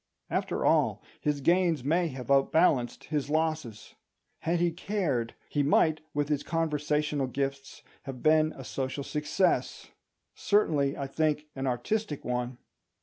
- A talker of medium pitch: Yes, medium, 150 Hz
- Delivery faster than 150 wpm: No, slow, 135 wpm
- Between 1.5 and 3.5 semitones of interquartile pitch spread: Yes, average, 2.8 semitones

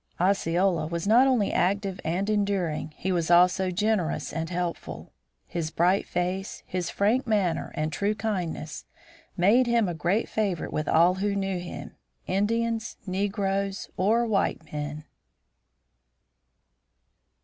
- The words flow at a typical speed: No, slow, 125 wpm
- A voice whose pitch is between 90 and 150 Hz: No, high, 190 Hz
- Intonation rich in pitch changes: No, average, 3.1 semitones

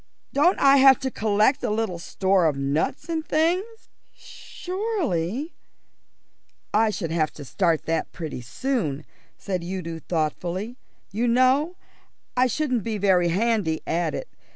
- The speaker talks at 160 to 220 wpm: No, average, 140 wpm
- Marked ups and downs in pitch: Yes, wide, 8.0 semitones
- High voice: Yes, high, 210 Hz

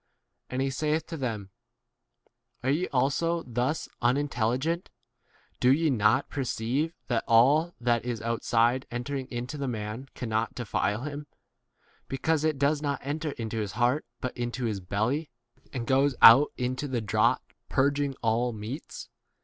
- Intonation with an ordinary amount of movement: Yes, average, 3.6 semitones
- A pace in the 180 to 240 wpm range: No, average, 155 wpm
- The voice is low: Yes, low, 130 Hz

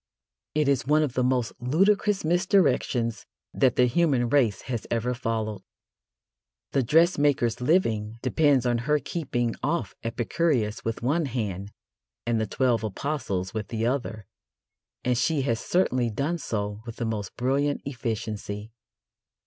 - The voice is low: Yes, low, 125 Hz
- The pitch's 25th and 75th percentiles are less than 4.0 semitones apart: No, average, 4.4 semitones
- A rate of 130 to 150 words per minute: Yes, average, 140 wpm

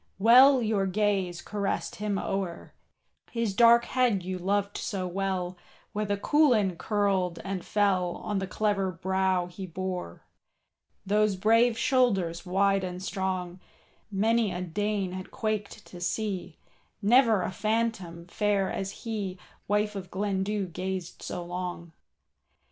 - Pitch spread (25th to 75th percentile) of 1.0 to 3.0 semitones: Yes, narrow, 2.5 semitones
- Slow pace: Yes, slow, 130 wpm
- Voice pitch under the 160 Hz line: No, high, 195 Hz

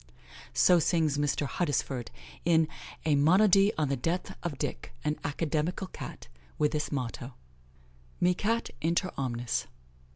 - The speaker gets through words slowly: Yes, slow, 130 wpm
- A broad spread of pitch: No, average, 4.0 semitones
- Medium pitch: Yes, medium, 155 Hz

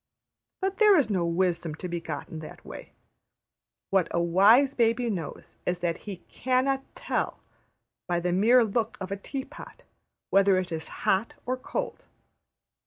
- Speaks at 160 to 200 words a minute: Yes, average, 165 wpm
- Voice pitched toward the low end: No, high, 195 Hz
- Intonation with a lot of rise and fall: Yes, wide, 6.4 semitones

